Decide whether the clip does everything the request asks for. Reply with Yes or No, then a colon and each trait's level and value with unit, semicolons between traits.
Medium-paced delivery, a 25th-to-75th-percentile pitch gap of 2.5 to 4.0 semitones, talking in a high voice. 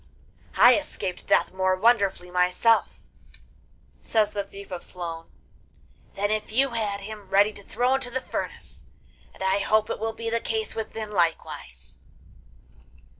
Yes: average, 150 wpm; average, 3.1 semitones; high, 210 Hz